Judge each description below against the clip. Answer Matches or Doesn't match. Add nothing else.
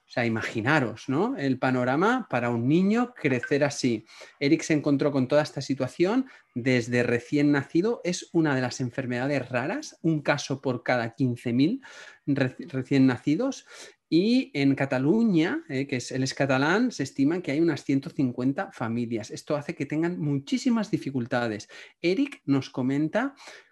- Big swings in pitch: Doesn't match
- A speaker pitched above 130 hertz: Matches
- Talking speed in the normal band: Matches